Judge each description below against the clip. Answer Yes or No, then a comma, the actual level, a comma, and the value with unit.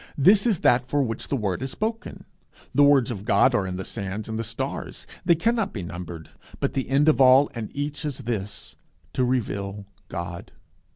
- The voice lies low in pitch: Yes, low, 125 Hz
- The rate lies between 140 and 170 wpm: No, average, 195 wpm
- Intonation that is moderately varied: No, wide, 6.1 semitones